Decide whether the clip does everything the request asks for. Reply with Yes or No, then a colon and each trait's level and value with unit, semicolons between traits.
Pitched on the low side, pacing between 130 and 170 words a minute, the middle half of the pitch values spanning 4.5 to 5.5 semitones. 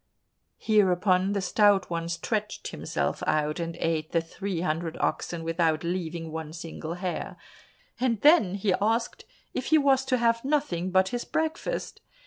No: medium, 185 Hz; average, 150 wpm; average, 5.1 semitones